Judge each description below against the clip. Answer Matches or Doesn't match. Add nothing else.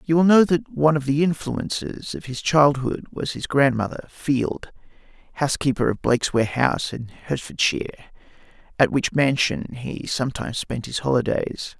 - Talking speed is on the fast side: Doesn't match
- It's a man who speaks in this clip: Matches